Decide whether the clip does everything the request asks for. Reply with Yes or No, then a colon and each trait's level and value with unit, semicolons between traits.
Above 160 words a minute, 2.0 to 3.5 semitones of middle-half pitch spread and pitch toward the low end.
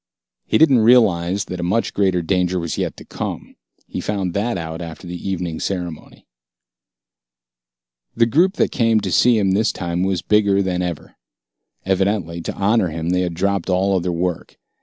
Yes: average, 175 wpm; average, 2.8 semitones; very low, 95 Hz